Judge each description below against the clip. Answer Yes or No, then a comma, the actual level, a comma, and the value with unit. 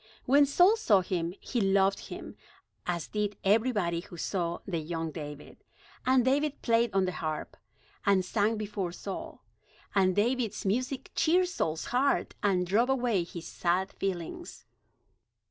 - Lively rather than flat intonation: Yes, wide, 5.7 semitones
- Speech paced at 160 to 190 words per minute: No, average, 145 wpm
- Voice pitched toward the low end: No, high, 200 Hz